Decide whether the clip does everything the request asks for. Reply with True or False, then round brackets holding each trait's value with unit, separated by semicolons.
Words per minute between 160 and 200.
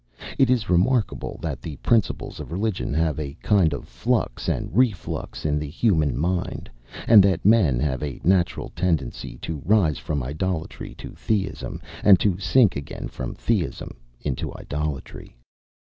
False (150 wpm)